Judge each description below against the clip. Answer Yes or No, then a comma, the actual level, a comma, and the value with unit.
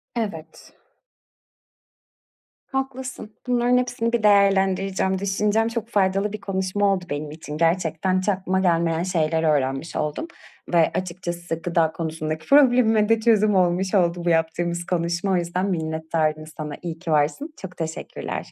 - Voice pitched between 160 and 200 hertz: Yes, medium, 185 Hz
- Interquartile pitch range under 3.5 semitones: No, average, 4.0 semitones